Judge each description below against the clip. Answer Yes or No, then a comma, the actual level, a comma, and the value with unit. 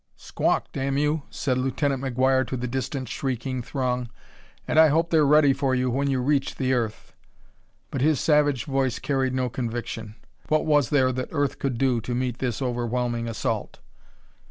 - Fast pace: No, average, 175 wpm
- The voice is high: No, low, 130 Hz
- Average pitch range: No, narrow, 2.2 semitones